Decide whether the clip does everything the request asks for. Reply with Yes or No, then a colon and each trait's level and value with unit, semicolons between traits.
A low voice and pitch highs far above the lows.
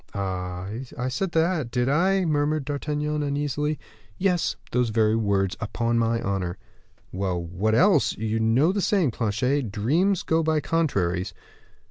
Yes: low, 125 Hz; wide, 6.9 semitones